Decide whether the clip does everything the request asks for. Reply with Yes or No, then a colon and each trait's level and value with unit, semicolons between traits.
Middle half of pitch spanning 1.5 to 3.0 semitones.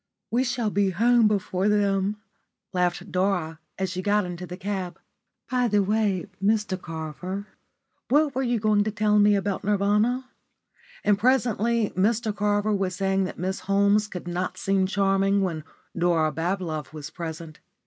Yes: narrow, 2.5 semitones